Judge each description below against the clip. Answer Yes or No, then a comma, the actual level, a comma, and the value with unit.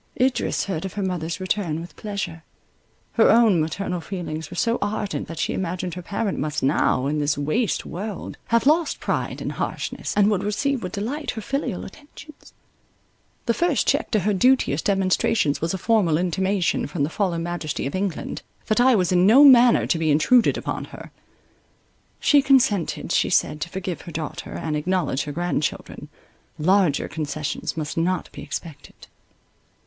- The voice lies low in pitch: No, medium, 185 Hz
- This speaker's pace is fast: No, average, 170 wpm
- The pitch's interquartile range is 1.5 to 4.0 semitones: No, average, 5.1 semitones